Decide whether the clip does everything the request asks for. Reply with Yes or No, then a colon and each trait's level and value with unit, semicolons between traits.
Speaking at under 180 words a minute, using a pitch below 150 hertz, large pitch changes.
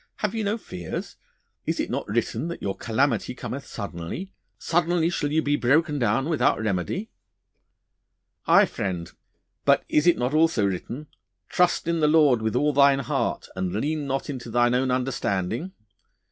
Yes: average, 160 wpm; low, 135 Hz; wide, 5.9 semitones